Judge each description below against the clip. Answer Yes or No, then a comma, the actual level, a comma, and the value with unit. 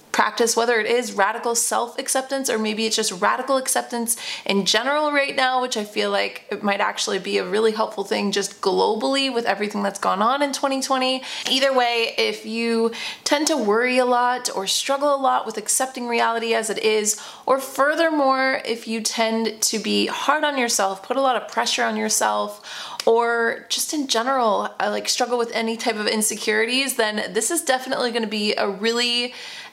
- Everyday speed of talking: Yes, average, 190 wpm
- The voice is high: Yes, high, 235 Hz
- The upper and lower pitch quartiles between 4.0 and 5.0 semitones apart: No, average, 3.5 semitones